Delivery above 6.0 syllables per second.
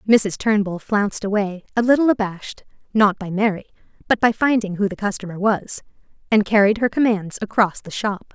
No: 5.4 syllables/s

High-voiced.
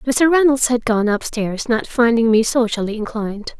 Yes: high, 235 Hz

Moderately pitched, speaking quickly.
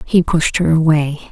No: medium, 160 Hz; average, 180 wpm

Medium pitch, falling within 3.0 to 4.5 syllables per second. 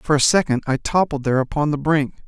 No: medium, 145 Hz; 6.2 syllables/s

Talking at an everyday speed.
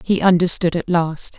Yes: average, 175 wpm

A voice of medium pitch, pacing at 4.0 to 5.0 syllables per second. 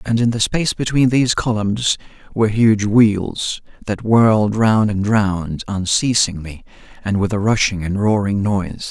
No: low, 105 Hz; 4.5 syllables/s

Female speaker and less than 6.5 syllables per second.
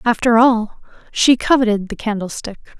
Yes: female; 4.9 syllables/s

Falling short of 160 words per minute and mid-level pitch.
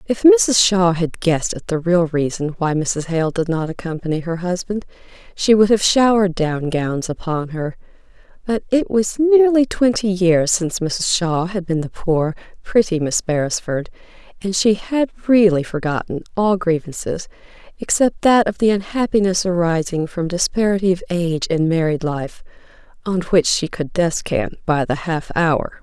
No: average, 165 wpm; medium, 180 Hz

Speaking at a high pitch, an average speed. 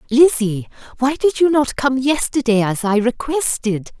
Yes: very high, 250 Hz; average, 150 wpm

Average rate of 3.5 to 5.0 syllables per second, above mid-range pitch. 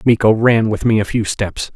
No: 4.9 syllables/s; low, 110 Hz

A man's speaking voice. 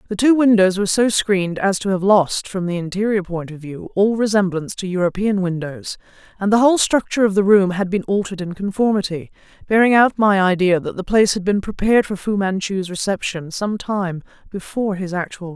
No: female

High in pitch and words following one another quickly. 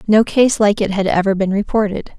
Yes: high, 205 Hz; fast, 220 wpm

